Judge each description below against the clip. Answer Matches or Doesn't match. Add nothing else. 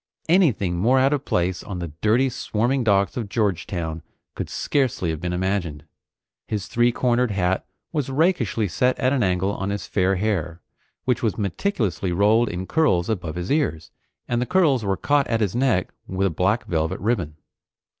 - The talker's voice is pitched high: Doesn't match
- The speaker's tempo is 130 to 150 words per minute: Doesn't match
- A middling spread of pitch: Doesn't match